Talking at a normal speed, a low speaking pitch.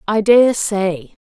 No: average, 145 wpm; high, 200 Hz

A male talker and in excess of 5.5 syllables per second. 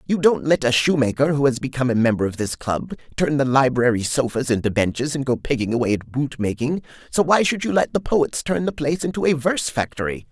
Yes: male; 6.0 syllables/s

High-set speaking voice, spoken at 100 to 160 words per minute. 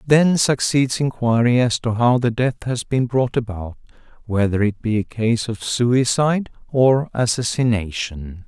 No: low, 120 Hz; average, 150 wpm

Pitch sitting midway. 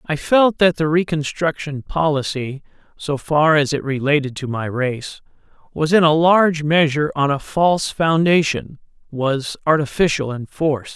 Yes: medium, 150 Hz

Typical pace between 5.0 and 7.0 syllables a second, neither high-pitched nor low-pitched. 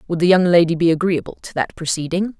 Yes: 6.3 syllables/s; medium, 170 Hz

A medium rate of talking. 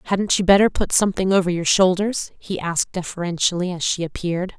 Yes: average, 185 wpm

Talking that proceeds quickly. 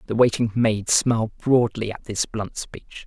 No: average, 175 wpm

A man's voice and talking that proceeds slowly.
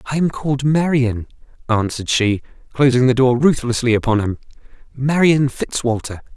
Yes: male; slow, 125 wpm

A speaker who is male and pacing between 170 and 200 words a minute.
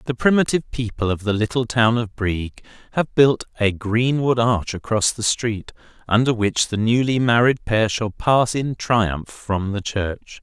Yes: male; average, 175 wpm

